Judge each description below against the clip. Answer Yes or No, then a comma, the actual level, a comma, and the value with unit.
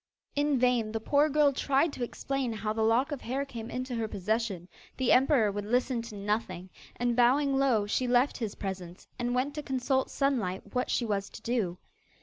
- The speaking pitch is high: Yes, high, 245 Hz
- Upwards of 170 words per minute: Yes, average, 195 wpm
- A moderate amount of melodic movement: Yes, average, 3.9 semitones